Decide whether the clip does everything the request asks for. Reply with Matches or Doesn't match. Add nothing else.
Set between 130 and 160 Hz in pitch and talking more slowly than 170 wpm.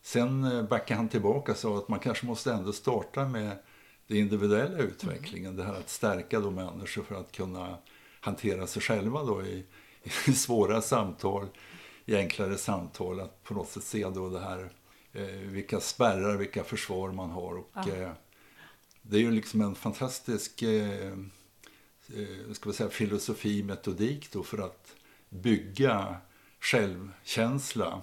Doesn't match